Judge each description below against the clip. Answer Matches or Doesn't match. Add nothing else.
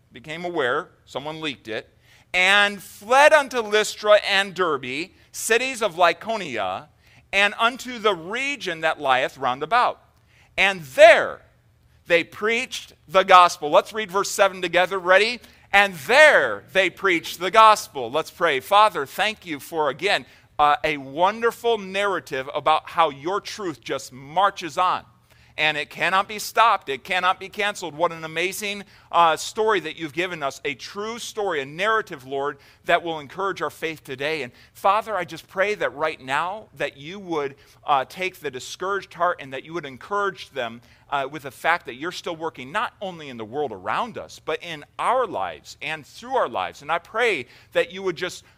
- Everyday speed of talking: Matches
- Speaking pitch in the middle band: Matches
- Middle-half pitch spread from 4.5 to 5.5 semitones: Matches